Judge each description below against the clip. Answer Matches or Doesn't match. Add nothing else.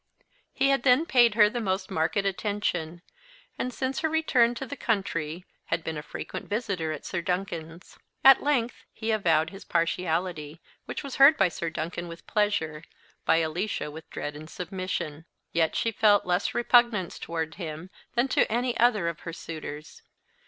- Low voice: Doesn't match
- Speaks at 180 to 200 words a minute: Doesn't match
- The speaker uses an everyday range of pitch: Doesn't match